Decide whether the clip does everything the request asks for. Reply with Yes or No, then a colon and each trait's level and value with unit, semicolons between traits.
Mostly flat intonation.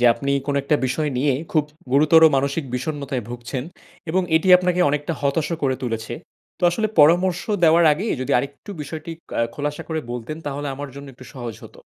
No: average, 3.3 semitones